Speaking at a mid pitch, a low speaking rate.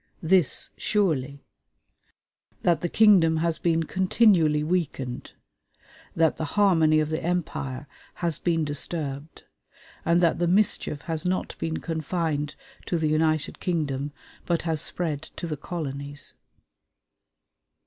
Yes: medium, 160 Hz; slow, 120 wpm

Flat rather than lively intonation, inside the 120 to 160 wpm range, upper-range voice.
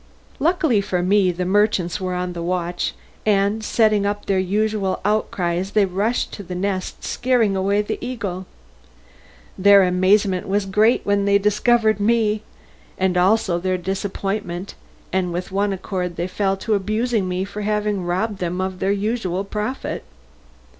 Yes: narrow, 2.3 semitones; average, 155 wpm; high, 200 Hz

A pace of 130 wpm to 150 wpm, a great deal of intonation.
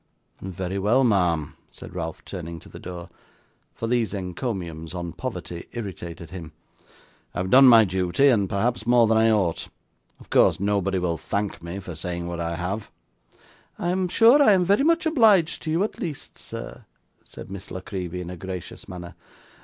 No: average, 180 wpm; wide, 5.8 semitones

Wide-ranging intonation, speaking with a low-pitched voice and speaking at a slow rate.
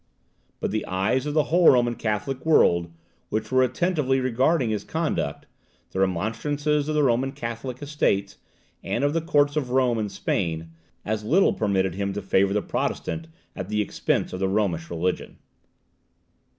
No: wide, 6.5 semitones; low, 115 Hz; average, 165 wpm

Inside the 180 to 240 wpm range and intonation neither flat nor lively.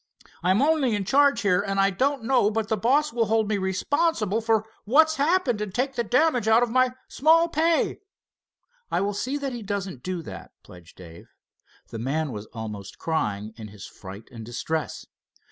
No: average, 185 wpm; wide, 8.6 semitones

